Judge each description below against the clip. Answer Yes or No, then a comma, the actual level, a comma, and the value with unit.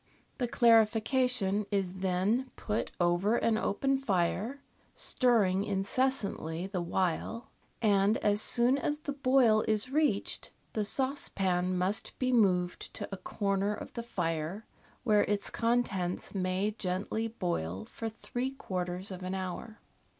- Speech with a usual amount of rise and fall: Yes, average, 4.3 semitones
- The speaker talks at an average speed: No, slow, 130 wpm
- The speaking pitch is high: Yes, high, 205 Hz